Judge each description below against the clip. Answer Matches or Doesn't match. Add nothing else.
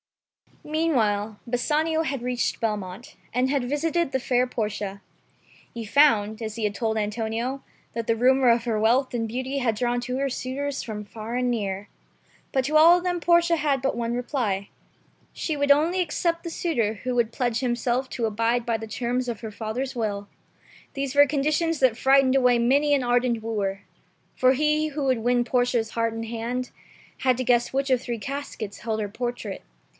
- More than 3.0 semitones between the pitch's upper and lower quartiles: Matches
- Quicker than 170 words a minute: Matches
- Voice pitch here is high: Matches